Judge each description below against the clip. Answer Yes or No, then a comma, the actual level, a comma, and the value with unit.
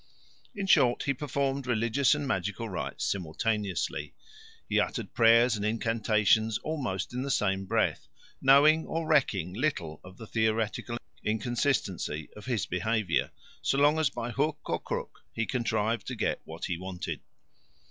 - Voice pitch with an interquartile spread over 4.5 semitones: Yes, average, 4.9 semitones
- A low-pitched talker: Yes, low, 115 Hz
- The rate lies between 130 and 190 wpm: Yes, average, 145 wpm